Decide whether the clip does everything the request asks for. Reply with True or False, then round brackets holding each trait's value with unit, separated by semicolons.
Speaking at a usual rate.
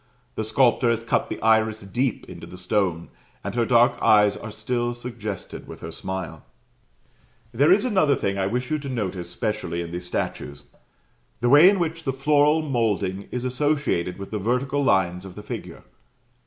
True (180 wpm)